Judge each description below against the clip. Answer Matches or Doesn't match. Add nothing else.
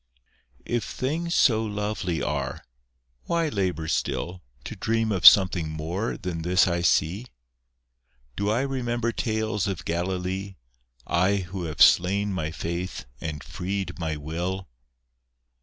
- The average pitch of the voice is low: Matches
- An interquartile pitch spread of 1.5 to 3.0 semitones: Doesn't match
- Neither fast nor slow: Doesn't match